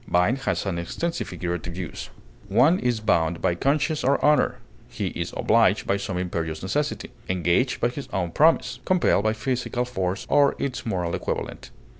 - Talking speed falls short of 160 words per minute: No, average, 165 wpm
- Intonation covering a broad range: Yes, wide, 7.7 semitones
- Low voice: Yes, low, 110 Hz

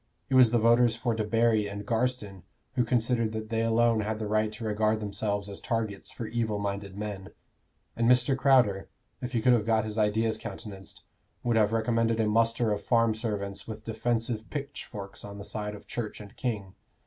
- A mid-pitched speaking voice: No, low, 110 Hz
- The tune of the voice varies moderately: No, narrow, 1.9 semitones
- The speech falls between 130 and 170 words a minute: No, average, 190 wpm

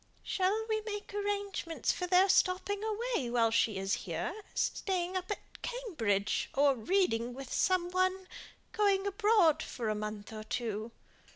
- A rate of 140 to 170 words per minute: Yes, average, 150 wpm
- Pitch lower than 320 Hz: No, very high, 365 Hz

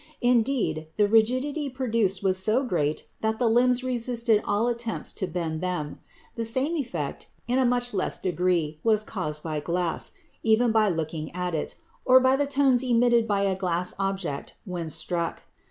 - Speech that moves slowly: No, average, 170 wpm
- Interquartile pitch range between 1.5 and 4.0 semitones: No, wide, 5.5 semitones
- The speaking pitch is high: Yes, high, 215 Hz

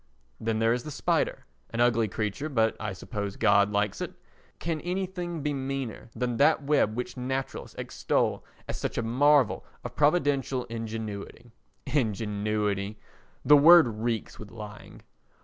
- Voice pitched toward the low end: Yes, low, 115 Hz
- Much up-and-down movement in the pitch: No, average, 4.7 semitones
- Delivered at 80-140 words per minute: Yes, slow, 135 wpm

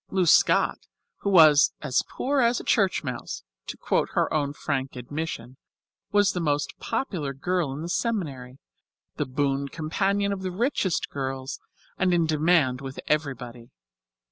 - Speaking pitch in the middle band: Yes, medium, 155 Hz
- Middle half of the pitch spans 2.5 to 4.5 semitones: No, wide, 5.6 semitones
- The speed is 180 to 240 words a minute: No, average, 150 wpm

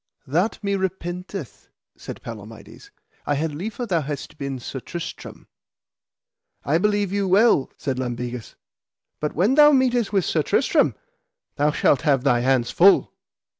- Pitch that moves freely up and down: Yes, wide, 6.9 semitones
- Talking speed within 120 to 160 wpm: Yes, average, 140 wpm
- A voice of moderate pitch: Yes, medium, 160 Hz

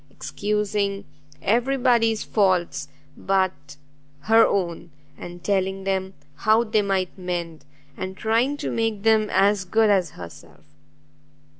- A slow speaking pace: Yes, slow, 120 wpm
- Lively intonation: No, average, 3.2 semitones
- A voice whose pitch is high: Yes, high, 195 Hz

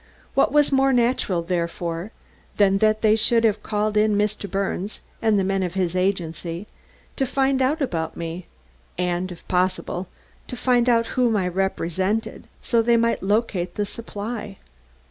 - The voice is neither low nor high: No, high, 205 Hz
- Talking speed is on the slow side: No, average, 160 wpm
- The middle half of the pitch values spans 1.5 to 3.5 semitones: No, average, 4.2 semitones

